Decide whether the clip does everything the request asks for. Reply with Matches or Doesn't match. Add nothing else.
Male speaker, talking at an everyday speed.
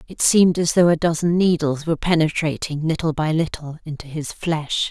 Doesn't match